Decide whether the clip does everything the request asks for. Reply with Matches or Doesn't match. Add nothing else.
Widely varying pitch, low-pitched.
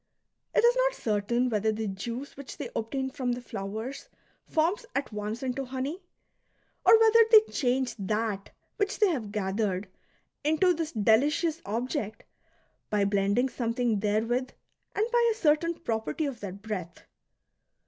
Doesn't match